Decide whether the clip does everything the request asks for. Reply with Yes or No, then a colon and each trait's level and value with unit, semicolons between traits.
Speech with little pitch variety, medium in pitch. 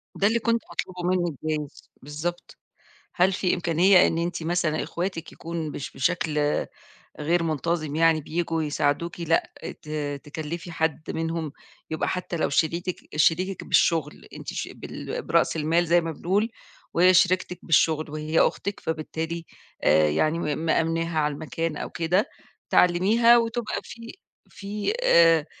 Yes: narrow, 2.3 semitones; medium, 165 Hz